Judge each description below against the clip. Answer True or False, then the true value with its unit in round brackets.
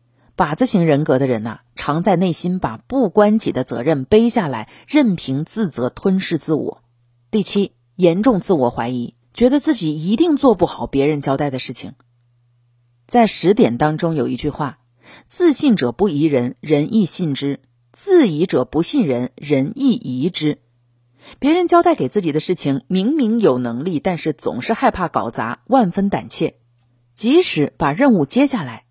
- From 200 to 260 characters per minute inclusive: True (245 characters per minute)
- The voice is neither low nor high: True (155 Hz)